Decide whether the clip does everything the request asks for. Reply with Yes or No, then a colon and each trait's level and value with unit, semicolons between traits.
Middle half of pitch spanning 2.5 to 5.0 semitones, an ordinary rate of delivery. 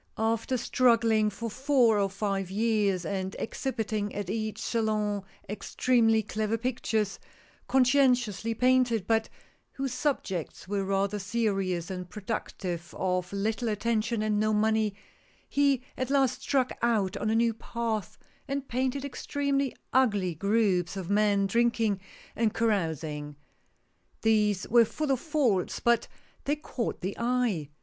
No: average, 3.4 semitones; slow, 130 wpm